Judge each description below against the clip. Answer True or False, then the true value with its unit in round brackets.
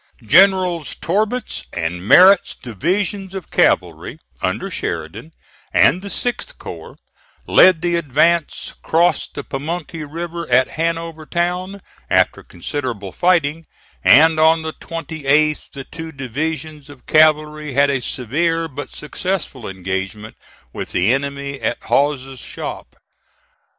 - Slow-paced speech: True (120 wpm)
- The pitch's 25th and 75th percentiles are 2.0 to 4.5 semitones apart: True (4.0 semitones)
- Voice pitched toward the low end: False (155 Hz)